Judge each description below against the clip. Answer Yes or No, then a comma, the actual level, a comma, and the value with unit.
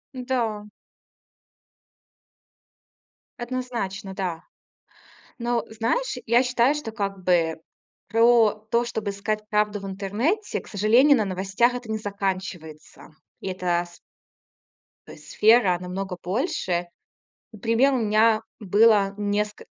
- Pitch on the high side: Yes, high, 210 Hz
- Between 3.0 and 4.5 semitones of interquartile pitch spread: Yes, average, 3.6 semitones